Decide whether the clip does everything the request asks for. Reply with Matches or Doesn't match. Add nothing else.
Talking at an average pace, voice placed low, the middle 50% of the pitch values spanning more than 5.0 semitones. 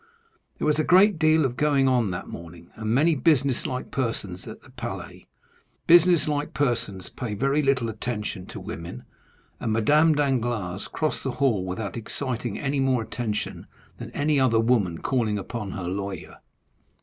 Matches